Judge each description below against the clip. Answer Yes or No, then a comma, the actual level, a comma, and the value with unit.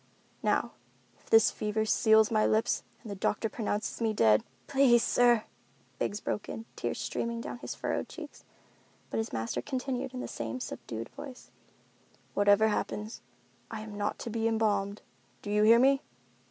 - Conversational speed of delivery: Yes, average, 160 wpm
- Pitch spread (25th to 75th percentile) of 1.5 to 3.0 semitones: Yes, narrow, 2.4 semitones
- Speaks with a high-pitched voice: Yes, high, 220 Hz